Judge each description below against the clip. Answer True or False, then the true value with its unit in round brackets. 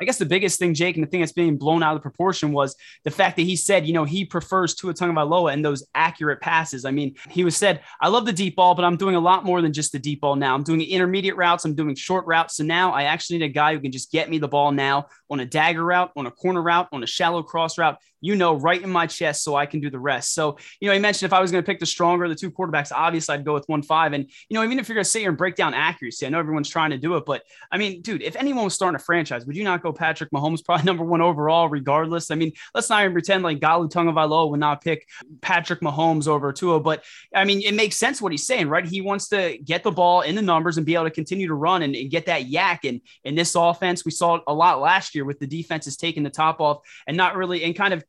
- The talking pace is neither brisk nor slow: False (300 wpm)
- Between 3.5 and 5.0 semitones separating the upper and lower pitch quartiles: False (3.1 semitones)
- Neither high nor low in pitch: True (165 Hz)